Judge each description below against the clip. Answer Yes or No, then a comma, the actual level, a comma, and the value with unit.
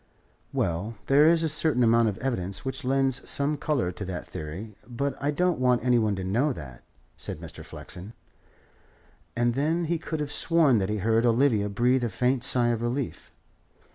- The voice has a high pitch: No, low, 120 Hz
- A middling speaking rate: Yes, average, 185 wpm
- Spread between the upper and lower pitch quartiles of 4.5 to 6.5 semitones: Yes, average, 4.9 semitones